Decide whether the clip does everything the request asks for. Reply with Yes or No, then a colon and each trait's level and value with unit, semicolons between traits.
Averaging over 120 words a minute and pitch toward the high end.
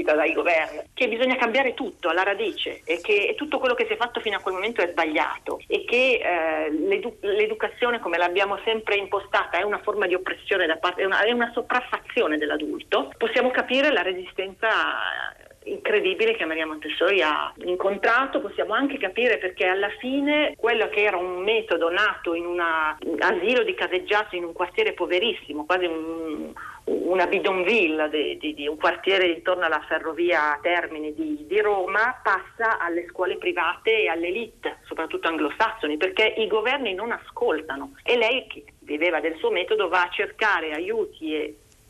Yes: average, 165 wpm; high, 210 Hz